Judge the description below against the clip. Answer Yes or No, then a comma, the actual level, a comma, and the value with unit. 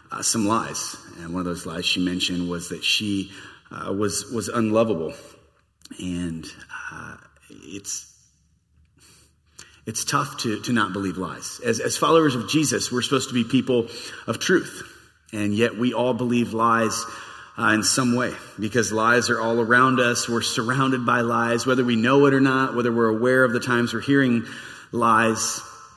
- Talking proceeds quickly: No, average, 170 wpm